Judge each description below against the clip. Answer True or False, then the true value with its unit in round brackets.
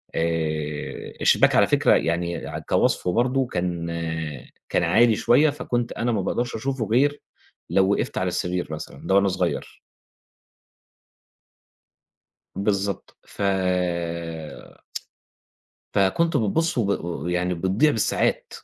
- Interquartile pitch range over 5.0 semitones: True (5.5 semitones)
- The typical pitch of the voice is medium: False (100 Hz)